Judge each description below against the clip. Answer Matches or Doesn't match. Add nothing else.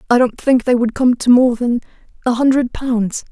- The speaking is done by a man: Doesn't match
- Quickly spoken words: Matches